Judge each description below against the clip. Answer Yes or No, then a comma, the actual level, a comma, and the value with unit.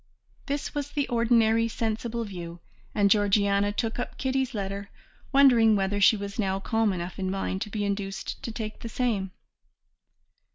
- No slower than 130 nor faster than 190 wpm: Yes, average, 160 wpm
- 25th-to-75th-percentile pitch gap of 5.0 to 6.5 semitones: No, average, 2.8 semitones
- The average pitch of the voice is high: Yes, high, 215 Hz